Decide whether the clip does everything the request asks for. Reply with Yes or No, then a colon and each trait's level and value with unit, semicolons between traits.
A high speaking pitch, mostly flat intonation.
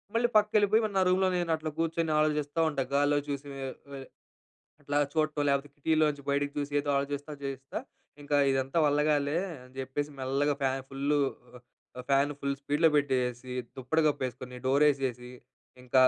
No: medium, 145 Hz; narrow, 2.1 semitones